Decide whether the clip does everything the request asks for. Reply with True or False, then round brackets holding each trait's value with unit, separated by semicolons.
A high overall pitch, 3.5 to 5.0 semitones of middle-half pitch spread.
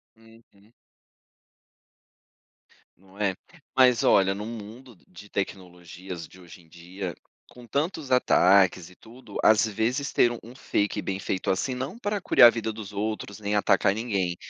False (105 Hz; 3.8 semitones)